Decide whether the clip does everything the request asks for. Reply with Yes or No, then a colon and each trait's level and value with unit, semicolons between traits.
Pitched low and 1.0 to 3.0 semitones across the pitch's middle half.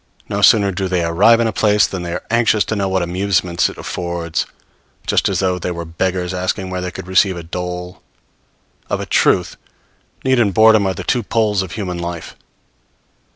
Yes: very low, 95 Hz; average, 2.7 semitones